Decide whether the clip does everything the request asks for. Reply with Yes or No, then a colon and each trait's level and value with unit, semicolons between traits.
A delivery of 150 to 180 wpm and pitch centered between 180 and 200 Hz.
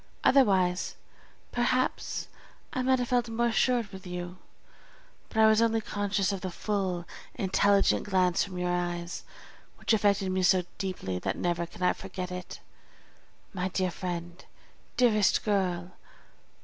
No: average, 140 wpm; high, 190 Hz